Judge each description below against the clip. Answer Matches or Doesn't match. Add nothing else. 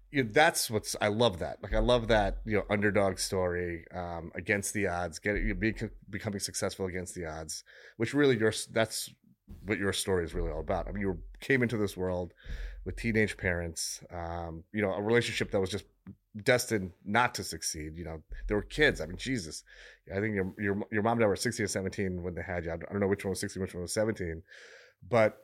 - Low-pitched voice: Matches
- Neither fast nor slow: Doesn't match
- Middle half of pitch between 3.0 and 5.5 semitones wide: Matches